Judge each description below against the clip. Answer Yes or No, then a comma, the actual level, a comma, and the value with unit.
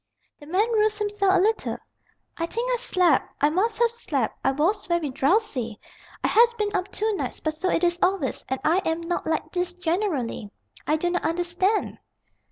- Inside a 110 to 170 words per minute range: No, average, 190 wpm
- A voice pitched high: Yes, very high, 360 Hz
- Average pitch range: Yes, average, 4.9 semitones